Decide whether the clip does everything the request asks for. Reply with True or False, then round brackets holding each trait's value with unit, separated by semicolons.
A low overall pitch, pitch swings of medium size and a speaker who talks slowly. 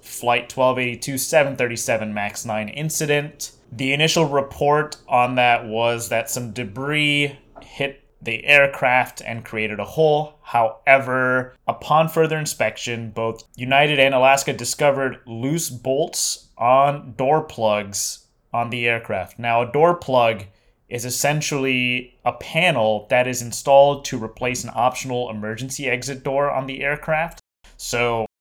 True (125 Hz; 3.3 semitones; 130 wpm)